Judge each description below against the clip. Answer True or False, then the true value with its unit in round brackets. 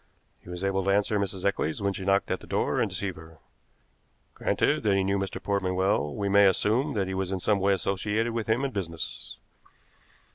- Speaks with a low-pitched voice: True (100 Hz)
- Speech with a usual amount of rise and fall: False (1.4 semitones)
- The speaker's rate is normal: False (215 wpm)